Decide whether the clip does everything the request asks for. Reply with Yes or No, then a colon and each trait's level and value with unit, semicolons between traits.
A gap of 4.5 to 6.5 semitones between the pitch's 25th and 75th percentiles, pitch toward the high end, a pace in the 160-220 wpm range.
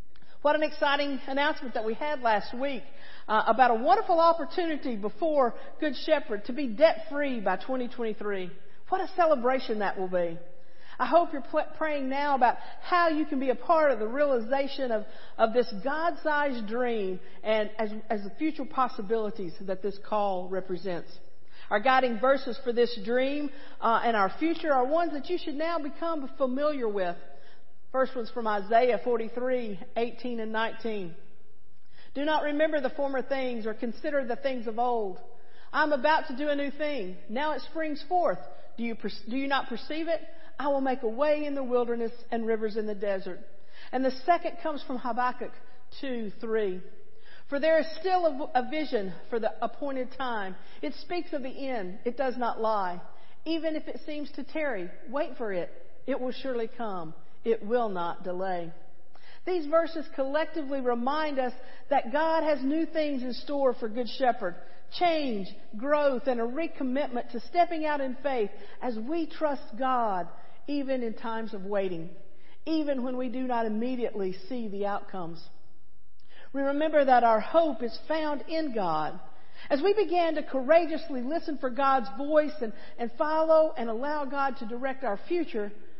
Yes: average, 5.2 semitones; very high, 255 Hz; average, 175 wpm